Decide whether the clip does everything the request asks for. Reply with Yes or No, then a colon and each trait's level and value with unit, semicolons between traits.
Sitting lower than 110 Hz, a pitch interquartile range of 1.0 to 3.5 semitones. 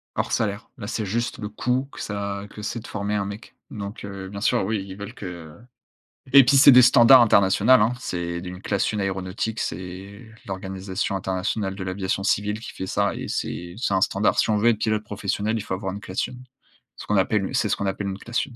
Yes: low, 100 Hz; narrow, 2.5 semitones